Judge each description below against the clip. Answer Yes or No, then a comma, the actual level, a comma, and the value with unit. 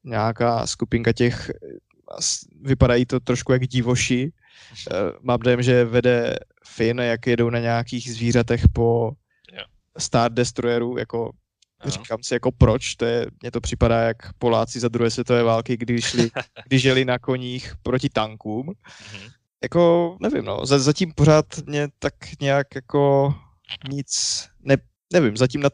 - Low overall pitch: Yes, low, 120 Hz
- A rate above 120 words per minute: Yes, average, 140 wpm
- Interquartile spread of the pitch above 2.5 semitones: No, narrow, 2.2 semitones